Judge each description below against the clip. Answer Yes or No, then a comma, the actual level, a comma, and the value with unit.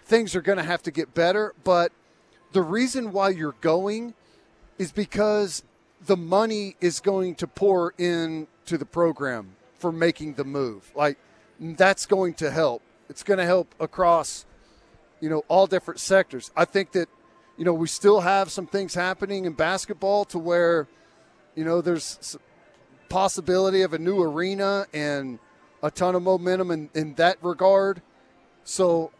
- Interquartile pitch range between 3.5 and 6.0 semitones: No, average, 3.0 semitones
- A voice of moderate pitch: Yes, medium, 175 Hz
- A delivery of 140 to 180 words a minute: Yes, average, 160 wpm